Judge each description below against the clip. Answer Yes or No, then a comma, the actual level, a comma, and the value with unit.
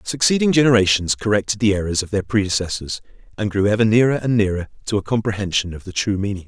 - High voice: No, low, 105 Hz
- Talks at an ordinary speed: Yes, average, 195 wpm